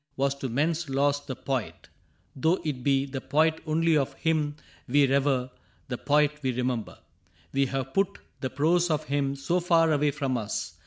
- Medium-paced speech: Yes, average, 180 wpm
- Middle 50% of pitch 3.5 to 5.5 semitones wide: No, average, 2.7 semitones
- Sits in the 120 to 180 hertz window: Yes, medium, 140 Hz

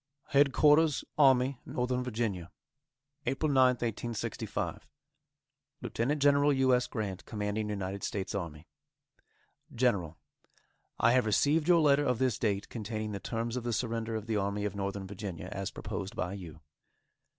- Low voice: Yes, low, 115 Hz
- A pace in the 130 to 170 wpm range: Yes, average, 140 wpm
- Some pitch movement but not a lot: Yes, average, 4.3 semitones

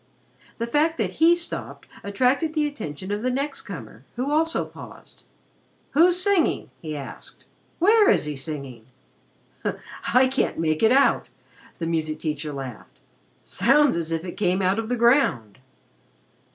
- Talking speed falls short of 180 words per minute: Yes, average, 145 wpm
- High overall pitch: Yes, high, 220 Hz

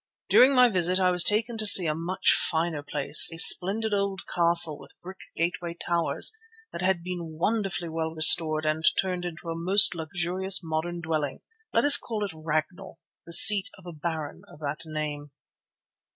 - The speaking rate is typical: Yes, average, 175 wpm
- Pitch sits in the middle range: Yes, medium, 170 Hz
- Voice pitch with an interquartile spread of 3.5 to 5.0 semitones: No, average, 3.1 semitones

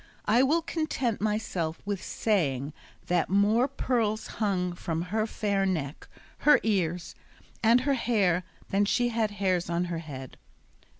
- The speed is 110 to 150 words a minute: Yes, average, 140 wpm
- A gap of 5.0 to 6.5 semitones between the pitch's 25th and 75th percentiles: No, average, 4.5 semitones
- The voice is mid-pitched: No, high, 200 Hz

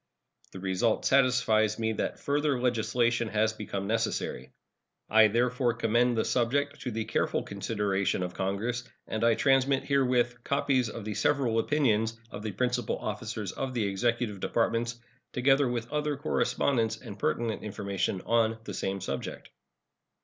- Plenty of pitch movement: No, average, 2.7 semitones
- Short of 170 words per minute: Yes, average, 145 wpm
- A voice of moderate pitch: No, low, 115 Hz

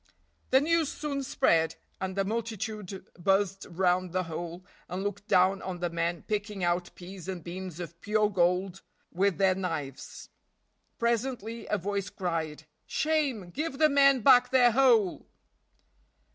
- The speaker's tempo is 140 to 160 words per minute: Yes, average, 145 wpm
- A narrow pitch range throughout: No, average, 4.7 semitones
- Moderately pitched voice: No, high, 195 Hz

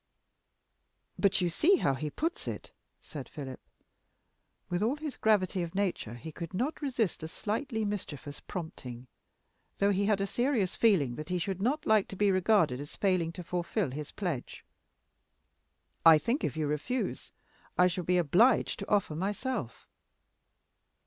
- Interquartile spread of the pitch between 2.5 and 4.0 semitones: No, wide, 5.4 semitones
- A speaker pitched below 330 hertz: Yes, medium, 185 Hz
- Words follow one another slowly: No, average, 155 wpm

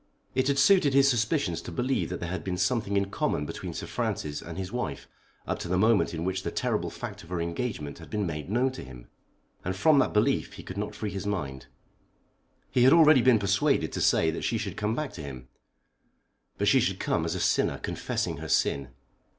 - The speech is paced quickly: Yes, fast, 225 wpm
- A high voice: No, low, 100 Hz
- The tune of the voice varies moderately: No, wide, 6.9 semitones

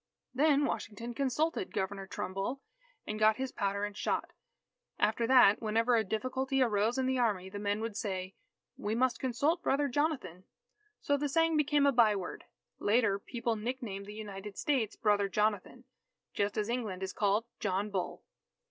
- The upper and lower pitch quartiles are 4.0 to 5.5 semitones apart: Yes, average, 4.3 semitones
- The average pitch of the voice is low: No, high, 220 Hz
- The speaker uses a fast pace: No, average, 160 wpm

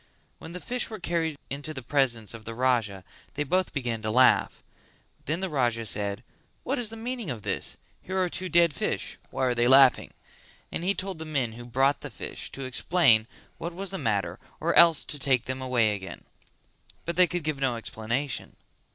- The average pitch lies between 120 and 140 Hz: Yes, low, 135 Hz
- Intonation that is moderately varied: No, wide, 6.5 semitones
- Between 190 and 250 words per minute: Yes, average, 200 wpm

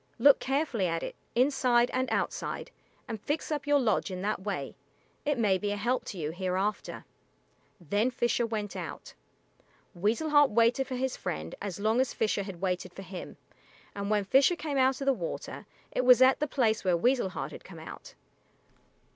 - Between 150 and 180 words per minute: No, average, 190 wpm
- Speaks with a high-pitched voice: Yes, high, 220 Hz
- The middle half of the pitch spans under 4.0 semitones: No, average, 5.3 semitones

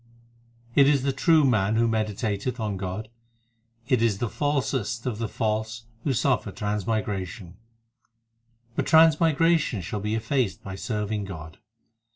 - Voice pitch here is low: Yes, low, 110 Hz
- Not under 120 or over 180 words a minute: Yes, slow, 135 wpm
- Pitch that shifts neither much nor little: Yes, average, 4.4 semitones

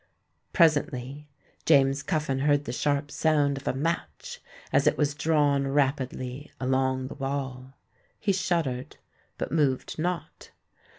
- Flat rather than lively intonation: Yes, narrow, 2.3 semitones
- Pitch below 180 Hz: Yes, medium, 140 Hz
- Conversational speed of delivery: No, slow, 120 wpm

